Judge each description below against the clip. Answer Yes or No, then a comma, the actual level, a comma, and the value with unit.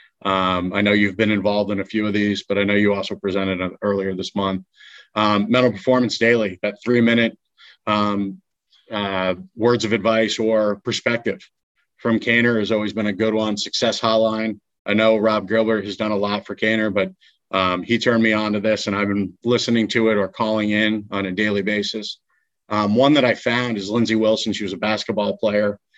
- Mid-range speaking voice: No, low, 105 Hz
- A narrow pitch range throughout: Yes, narrow, 1.7 semitones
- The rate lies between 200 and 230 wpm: Yes, fast, 205 wpm